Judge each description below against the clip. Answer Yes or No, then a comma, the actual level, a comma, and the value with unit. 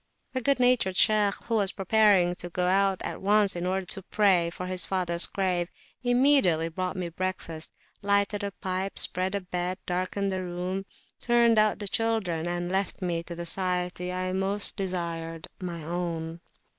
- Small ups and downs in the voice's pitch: Yes, narrow, 2.3 semitones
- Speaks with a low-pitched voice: No, medium, 185 Hz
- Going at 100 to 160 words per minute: No, average, 170 wpm